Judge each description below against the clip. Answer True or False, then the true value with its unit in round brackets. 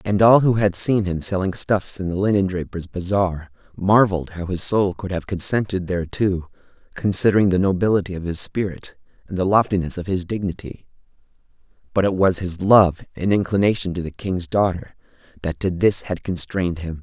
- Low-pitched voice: True (95 Hz)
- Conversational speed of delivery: True (175 wpm)